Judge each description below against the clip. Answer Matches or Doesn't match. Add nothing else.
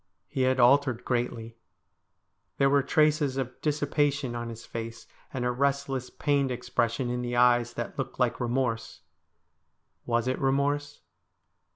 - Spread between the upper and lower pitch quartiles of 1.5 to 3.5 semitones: Matches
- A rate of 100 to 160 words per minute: Matches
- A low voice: Matches